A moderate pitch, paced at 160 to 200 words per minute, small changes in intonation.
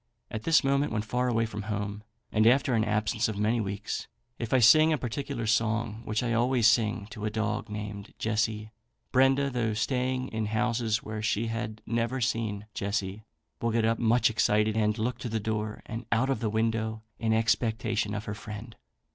No: low, 110 Hz; average, 190 wpm; narrow, 1.8 semitones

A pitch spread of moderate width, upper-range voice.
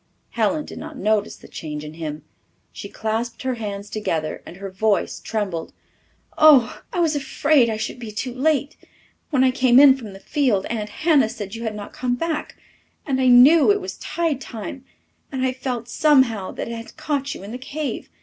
Yes: average, 4.9 semitones; high, 245 Hz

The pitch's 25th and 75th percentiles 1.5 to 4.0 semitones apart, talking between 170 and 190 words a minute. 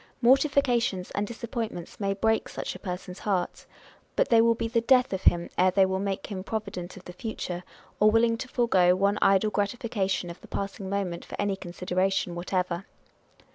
Yes: average, 3.6 semitones; average, 180 wpm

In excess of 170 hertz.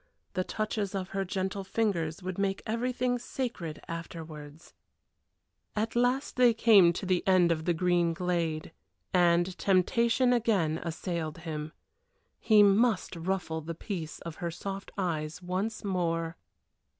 Yes: medium, 185 Hz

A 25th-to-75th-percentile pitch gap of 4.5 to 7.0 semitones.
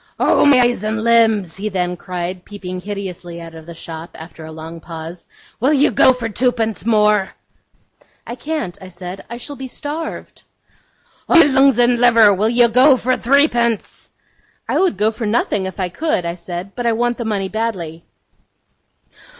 Yes: average, 5.2 semitones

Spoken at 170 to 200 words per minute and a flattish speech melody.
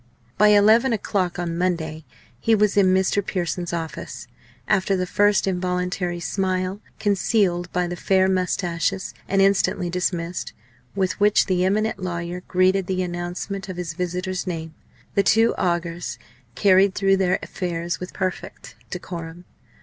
No: average, 140 wpm; narrow, 1.8 semitones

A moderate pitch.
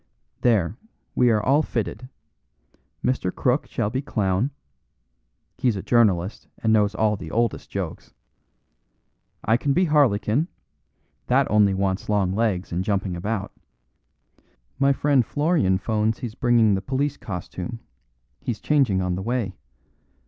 No: low, 110 Hz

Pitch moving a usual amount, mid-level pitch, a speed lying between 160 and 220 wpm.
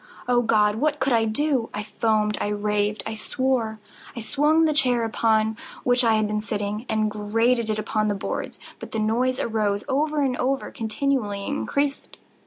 No: average, 3.4 semitones; high, 225 Hz; average, 170 wpm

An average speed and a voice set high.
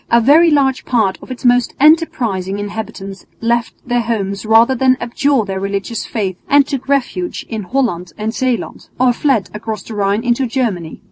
Yes: average, 175 wpm; high, 235 Hz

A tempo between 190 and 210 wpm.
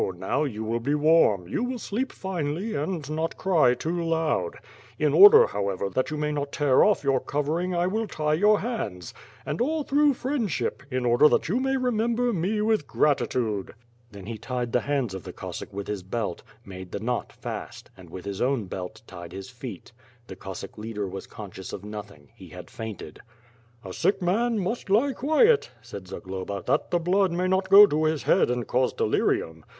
Yes: average, 195 wpm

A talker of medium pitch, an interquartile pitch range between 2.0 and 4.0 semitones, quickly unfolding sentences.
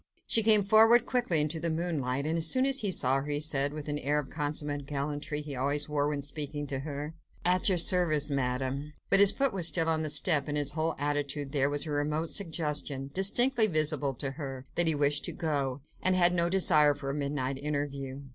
Yes: medium, 150 Hz; average, 2.9 semitones; fast, 220 wpm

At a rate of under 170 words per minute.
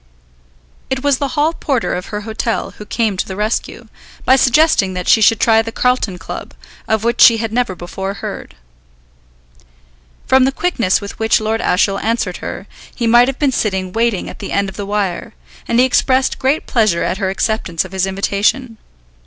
No: average, 190 wpm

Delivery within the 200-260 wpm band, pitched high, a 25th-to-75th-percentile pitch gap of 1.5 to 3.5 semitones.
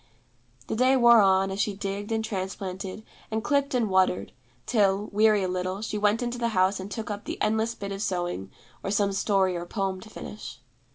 Yes: fast, 205 wpm; high, 200 Hz; narrow, 2.5 semitones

